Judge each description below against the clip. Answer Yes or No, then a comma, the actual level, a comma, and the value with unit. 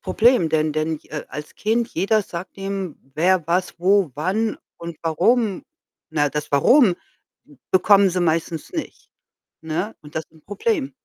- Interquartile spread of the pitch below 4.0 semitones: No, average, 4.7 semitones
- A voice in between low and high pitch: Yes, medium, 180 Hz